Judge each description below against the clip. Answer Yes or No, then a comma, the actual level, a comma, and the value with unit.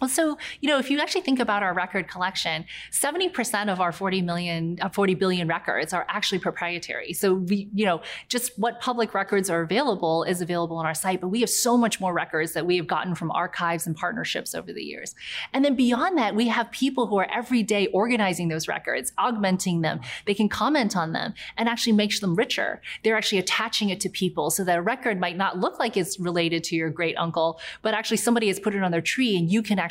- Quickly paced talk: Yes, fast, 235 wpm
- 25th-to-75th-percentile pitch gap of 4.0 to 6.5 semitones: Yes, average, 4.8 semitones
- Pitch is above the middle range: Yes, high, 195 Hz